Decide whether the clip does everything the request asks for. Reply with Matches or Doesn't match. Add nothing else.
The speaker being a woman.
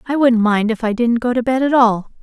Matches